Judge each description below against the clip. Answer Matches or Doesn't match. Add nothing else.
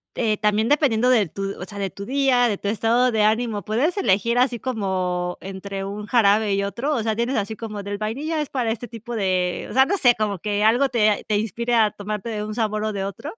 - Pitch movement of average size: Matches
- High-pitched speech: Matches